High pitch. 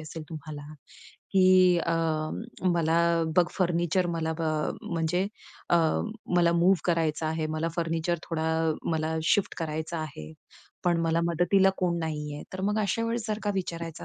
No: medium, 165 Hz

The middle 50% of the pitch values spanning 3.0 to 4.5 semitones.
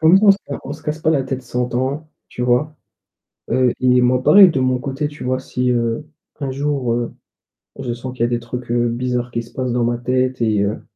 No: narrow, 2.5 semitones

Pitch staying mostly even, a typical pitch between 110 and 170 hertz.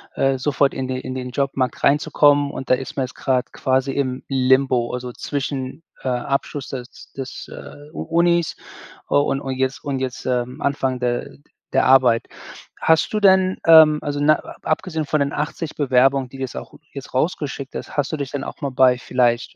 Yes: narrow, 2.1 semitones; low, 135 Hz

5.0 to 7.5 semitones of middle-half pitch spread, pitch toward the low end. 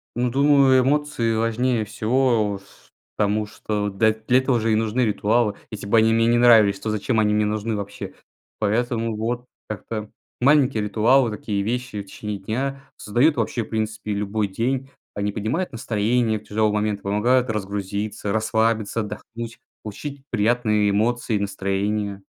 No: narrow, 2.6 semitones; low, 110 Hz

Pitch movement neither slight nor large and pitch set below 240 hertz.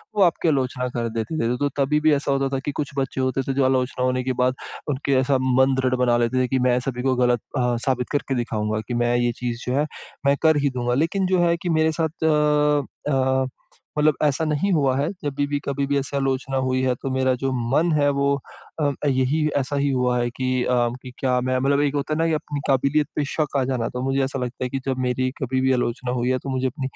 No: narrow, 2.1 semitones; low, 135 Hz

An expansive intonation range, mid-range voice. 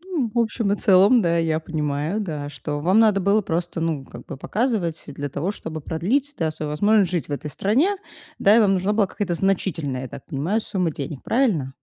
Yes: wide, 5.8 semitones; medium, 175 Hz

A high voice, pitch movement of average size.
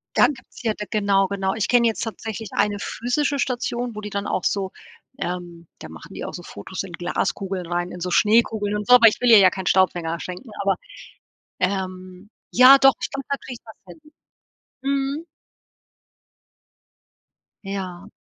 Yes: high, 205 Hz; average, 4.4 semitones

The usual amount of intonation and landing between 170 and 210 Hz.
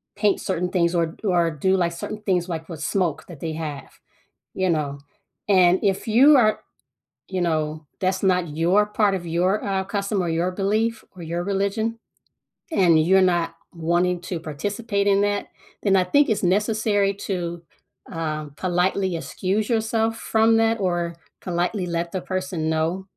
Yes: average, 3.0 semitones; medium, 185 Hz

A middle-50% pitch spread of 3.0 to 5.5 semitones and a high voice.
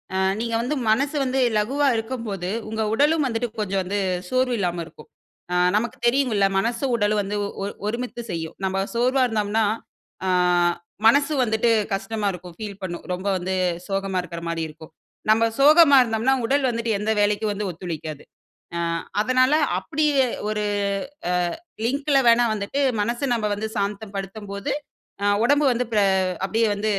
Yes: average, 4.2 semitones; high, 220 Hz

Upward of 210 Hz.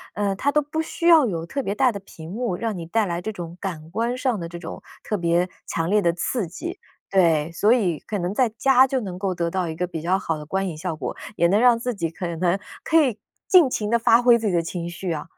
No: high, 195 Hz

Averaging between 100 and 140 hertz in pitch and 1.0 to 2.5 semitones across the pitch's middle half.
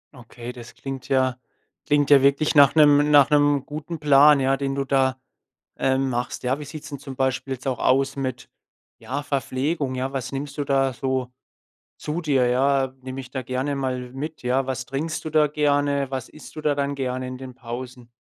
Yes: low, 135 Hz; narrow, 1.9 semitones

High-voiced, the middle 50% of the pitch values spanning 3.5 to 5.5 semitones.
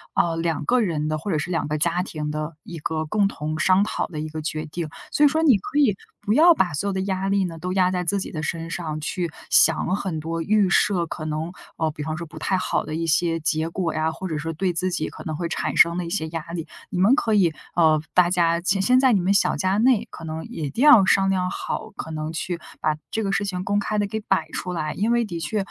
No: medium, 175 Hz; average, 3.8 semitones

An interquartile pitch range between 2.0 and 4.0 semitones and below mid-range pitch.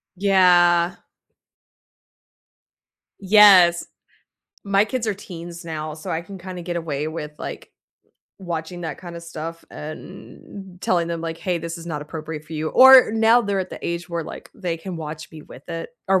No: average, 2.7 semitones; medium, 170 Hz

